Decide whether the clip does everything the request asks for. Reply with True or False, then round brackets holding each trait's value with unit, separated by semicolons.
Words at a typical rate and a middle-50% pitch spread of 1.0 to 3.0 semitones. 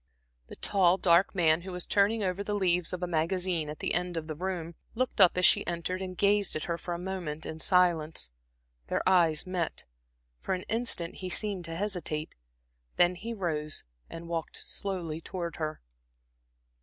True (180 wpm; 2.5 semitones)